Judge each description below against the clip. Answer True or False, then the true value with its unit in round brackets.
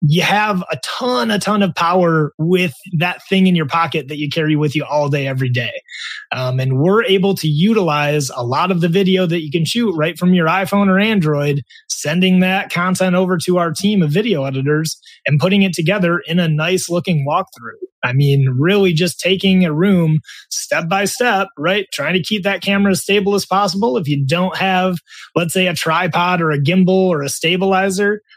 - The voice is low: False (180 Hz)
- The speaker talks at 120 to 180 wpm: False (205 wpm)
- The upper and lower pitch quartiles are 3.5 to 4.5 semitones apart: True (3.8 semitones)